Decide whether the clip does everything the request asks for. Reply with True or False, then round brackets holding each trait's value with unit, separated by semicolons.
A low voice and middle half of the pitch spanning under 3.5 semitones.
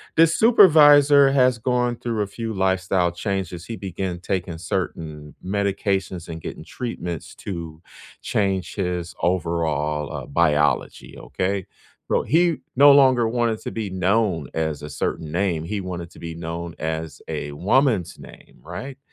False (95 Hz; 5.6 semitones)